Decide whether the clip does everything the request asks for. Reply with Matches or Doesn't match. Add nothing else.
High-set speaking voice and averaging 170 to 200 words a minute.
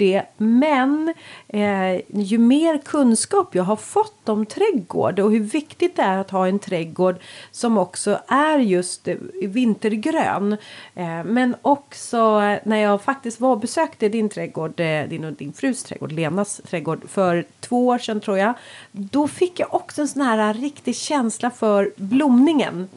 Doesn't match